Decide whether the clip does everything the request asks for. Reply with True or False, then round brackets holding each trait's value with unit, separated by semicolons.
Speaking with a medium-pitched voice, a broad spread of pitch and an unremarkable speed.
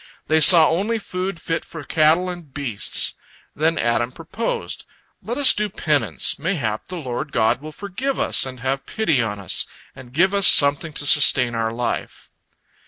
True (155 Hz; 6.2 semitones; 170 wpm)